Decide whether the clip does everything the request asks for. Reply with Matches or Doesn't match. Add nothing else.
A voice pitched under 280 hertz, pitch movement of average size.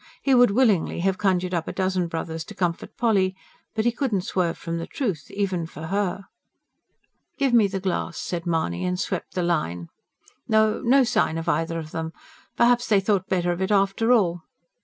Matches